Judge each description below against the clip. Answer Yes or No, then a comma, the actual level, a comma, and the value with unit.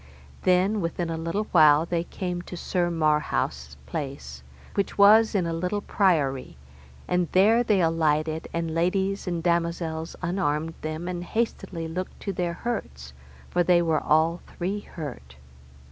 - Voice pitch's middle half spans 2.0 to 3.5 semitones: Yes, average, 2.7 semitones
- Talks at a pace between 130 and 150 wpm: Yes, average, 145 wpm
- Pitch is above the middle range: No, medium, 170 Hz